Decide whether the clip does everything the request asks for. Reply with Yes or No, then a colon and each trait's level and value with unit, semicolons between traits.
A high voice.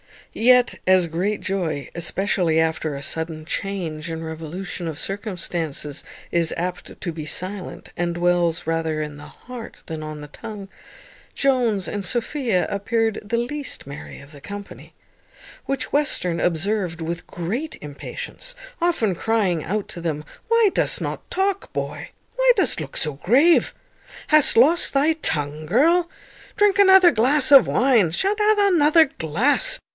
Yes: high, 195 Hz